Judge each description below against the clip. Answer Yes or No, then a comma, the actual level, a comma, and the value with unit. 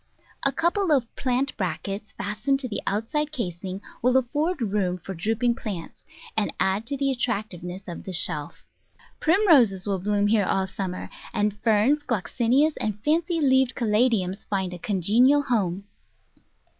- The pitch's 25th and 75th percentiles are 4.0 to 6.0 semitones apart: Yes, wide, 5.5 semitones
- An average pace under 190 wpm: Yes, average, 145 wpm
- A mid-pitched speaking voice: No, high, 215 Hz